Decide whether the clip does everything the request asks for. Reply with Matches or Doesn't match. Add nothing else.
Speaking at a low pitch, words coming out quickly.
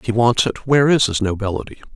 Matches